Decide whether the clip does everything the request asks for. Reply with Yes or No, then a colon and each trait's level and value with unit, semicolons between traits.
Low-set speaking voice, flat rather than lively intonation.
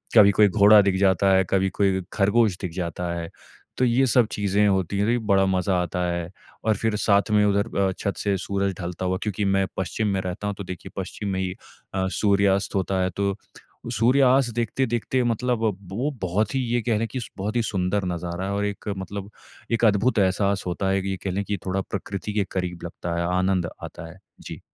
Yes: low, 100 Hz; narrow, 2.1 semitones